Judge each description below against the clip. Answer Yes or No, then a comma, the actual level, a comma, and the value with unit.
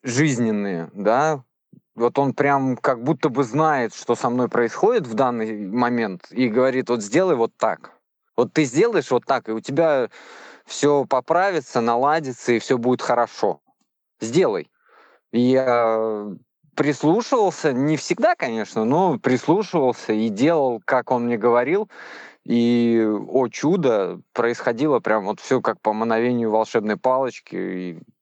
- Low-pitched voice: Yes, low, 125 Hz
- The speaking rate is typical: Yes, average, 140 wpm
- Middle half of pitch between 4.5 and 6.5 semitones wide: No, average, 3.5 semitones